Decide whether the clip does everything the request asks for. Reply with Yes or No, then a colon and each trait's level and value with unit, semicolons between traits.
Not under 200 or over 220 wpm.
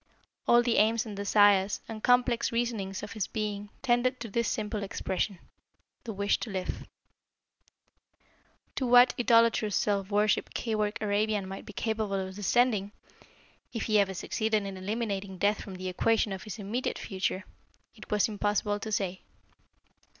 No: average, 150 wpm